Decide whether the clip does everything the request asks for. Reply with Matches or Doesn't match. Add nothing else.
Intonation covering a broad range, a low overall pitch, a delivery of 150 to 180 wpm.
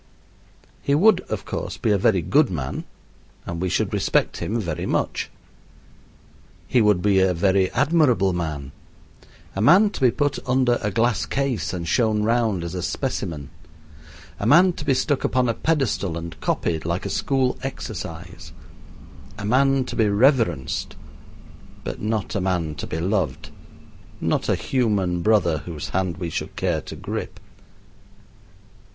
Matches